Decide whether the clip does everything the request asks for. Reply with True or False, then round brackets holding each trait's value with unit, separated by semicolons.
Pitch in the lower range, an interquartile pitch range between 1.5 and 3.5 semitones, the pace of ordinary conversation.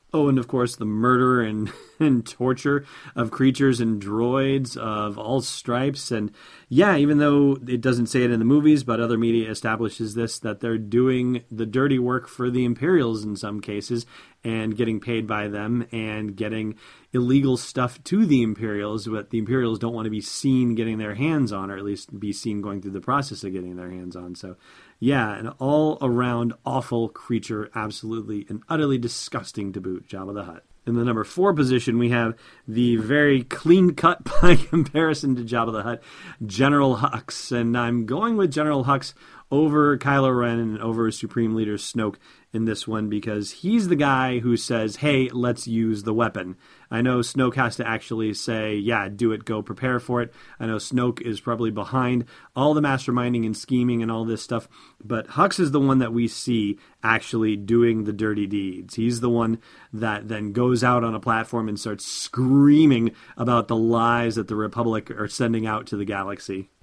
True (115 Hz; 2.9 semitones; 190 wpm)